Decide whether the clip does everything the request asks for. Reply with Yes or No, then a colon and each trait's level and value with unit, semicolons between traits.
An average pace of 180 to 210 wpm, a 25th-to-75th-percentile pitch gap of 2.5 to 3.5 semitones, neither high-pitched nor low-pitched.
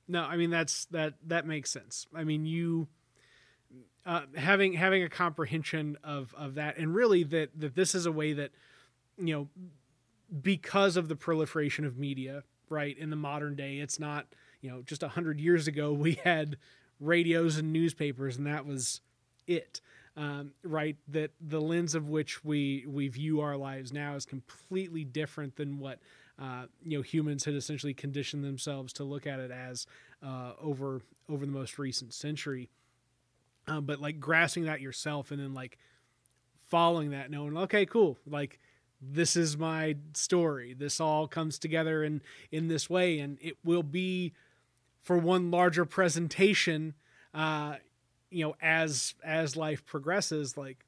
No: average, 165 wpm; average, 2.8 semitones; medium, 150 Hz